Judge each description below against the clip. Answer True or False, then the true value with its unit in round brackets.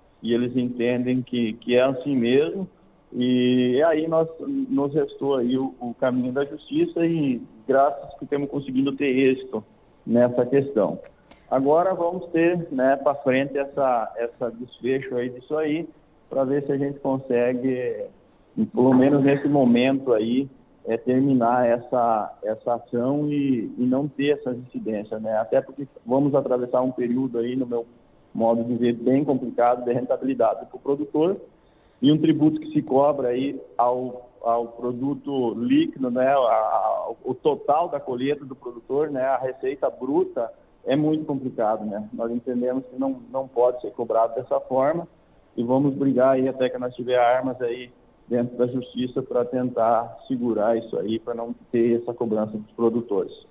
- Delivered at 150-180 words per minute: True (165 wpm)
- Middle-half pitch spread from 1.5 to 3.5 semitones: True (2.7 semitones)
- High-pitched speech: False (130 Hz)